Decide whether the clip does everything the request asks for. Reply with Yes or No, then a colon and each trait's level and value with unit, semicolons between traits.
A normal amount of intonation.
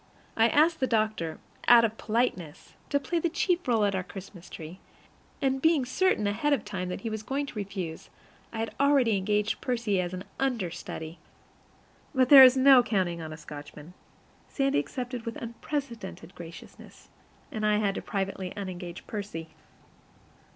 No: wide, 6.0 semitones